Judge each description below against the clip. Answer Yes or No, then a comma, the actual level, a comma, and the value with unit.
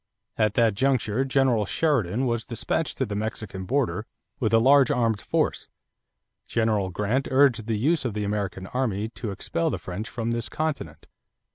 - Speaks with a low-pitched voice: Yes, low, 115 Hz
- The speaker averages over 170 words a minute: No, average, 165 wpm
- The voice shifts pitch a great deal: No, average, 3.9 semitones